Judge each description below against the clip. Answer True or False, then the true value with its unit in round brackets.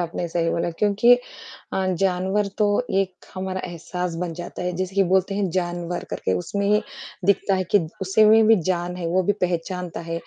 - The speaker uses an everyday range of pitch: False (2.0 semitones)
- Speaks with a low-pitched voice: False (185 Hz)